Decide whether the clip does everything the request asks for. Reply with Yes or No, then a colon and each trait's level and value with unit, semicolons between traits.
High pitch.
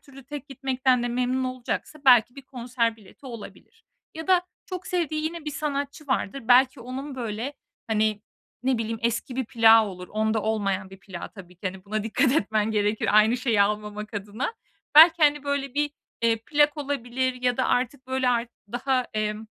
Yes: high, 245 Hz